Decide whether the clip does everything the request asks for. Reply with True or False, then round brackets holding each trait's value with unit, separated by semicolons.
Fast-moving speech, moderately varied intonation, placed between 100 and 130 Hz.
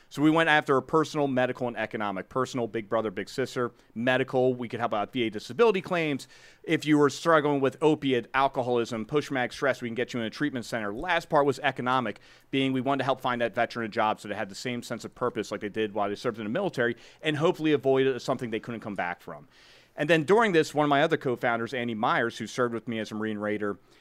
True (250 wpm; 3.8 semitones; 125 Hz)